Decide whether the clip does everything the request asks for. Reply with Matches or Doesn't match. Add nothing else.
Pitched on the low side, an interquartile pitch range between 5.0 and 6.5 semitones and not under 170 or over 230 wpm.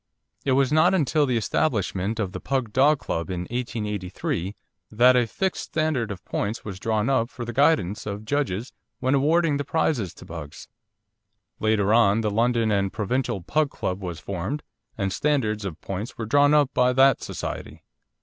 Matches